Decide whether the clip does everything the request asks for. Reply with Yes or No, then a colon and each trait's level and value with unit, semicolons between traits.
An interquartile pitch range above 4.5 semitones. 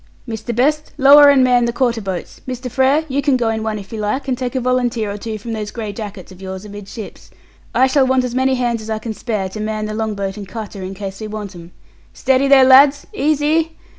No: average, 3.8 semitones